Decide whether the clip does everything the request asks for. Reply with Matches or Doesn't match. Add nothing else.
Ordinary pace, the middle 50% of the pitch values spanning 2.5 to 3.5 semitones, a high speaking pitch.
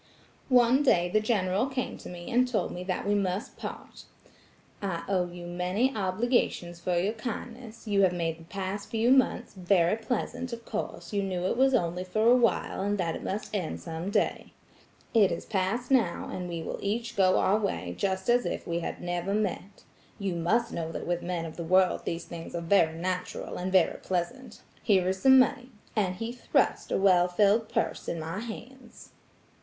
Doesn't match